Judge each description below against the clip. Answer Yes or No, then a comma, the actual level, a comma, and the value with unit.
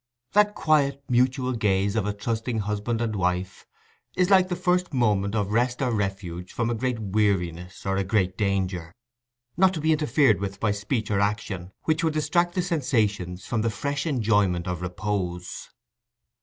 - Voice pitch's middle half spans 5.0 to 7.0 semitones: Yes, wide, 5.5 semitones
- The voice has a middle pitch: No, low, 110 Hz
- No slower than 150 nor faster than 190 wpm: Yes, average, 170 wpm